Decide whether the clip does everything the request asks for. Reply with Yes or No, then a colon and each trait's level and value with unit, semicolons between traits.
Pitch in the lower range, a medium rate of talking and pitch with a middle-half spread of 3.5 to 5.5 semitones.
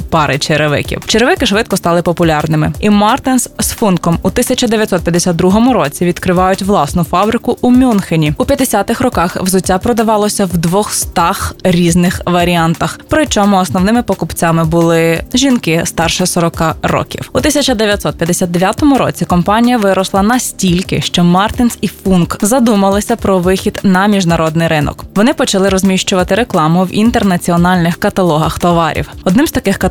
No: high, 190 Hz; average, 125 wpm; average, 4.0 semitones